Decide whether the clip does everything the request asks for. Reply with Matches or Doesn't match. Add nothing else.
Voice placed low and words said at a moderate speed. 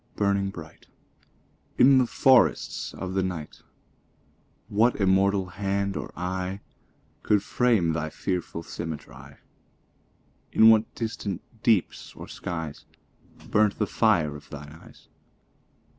Doesn't match